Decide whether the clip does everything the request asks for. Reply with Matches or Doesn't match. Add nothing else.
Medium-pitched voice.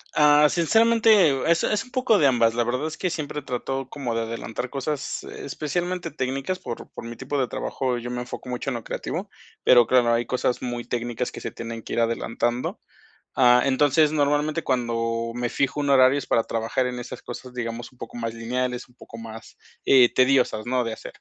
Doesn't match